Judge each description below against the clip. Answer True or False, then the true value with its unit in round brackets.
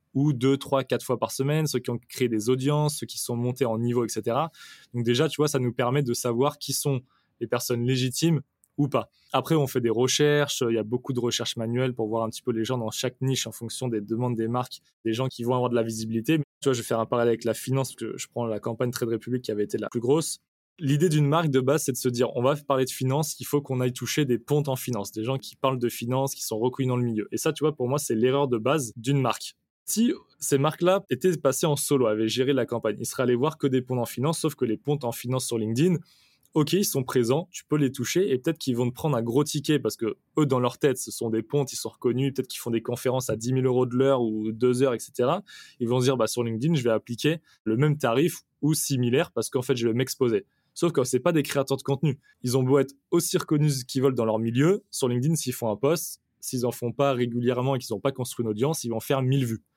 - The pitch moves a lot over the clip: False (3.2 semitones)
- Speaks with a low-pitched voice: True (130 Hz)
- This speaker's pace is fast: True (280 wpm)